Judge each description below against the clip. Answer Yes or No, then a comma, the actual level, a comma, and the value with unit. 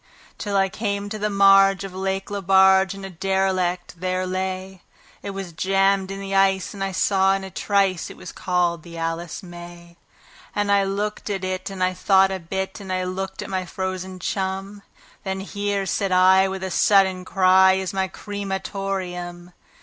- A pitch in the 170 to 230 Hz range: Yes, high, 190 Hz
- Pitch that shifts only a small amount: Yes, narrow, 1.1 semitones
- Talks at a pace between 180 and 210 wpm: Yes, average, 190 wpm